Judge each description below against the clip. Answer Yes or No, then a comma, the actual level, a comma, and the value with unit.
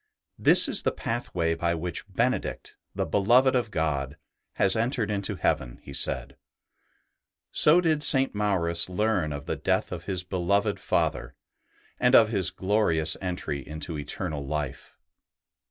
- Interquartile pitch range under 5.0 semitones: No, wide, 5.6 semitones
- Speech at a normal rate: Yes, average, 145 wpm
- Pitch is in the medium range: No, very low, 90 Hz